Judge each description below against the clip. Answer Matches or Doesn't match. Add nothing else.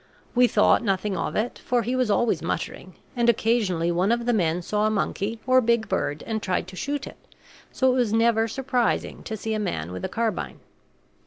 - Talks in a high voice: Matches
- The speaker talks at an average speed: Doesn't match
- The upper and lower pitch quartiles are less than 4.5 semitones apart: Matches